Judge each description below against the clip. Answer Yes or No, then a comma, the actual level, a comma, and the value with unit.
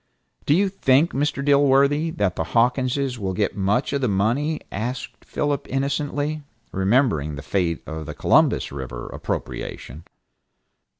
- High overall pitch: No, low, 125 Hz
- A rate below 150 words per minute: Yes, slow, 135 wpm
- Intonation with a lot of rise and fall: Yes, wide, 7.0 semitones